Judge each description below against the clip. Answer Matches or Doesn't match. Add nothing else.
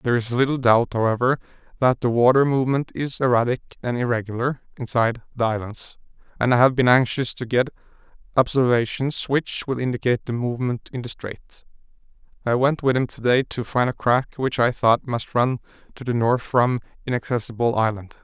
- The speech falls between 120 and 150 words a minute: Doesn't match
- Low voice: Matches